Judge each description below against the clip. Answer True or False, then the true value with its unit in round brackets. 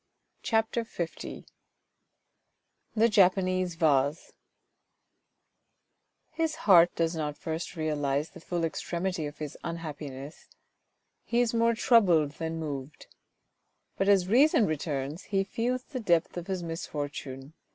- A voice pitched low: False (170 Hz)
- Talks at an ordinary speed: False (120 wpm)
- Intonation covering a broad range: False (4.8 semitones)